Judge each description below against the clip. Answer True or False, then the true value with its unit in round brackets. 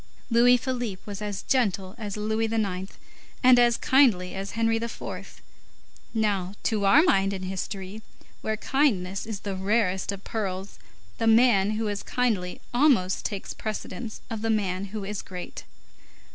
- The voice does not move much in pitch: False (3.0 semitones)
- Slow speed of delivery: False (150 wpm)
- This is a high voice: True (210 Hz)